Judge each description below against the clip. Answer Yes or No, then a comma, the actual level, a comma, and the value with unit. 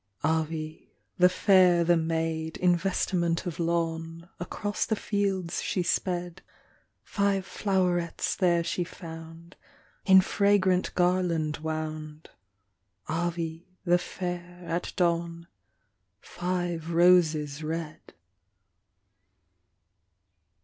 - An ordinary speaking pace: No, slow, 90 wpm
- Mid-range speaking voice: Yes, medium, 170 Hz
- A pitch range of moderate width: No, narrow, 1.8 semitones